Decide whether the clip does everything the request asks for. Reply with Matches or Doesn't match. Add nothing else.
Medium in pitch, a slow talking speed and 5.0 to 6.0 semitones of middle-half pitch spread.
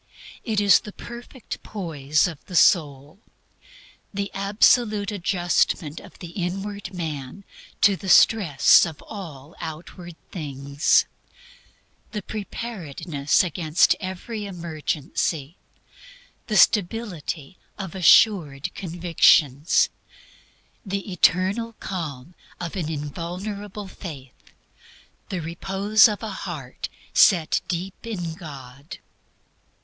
Doesn't match